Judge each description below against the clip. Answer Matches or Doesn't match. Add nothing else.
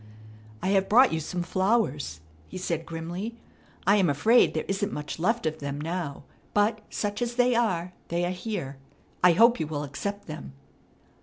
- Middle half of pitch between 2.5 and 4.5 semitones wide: Doesn't match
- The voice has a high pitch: Doesn't match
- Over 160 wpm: Matches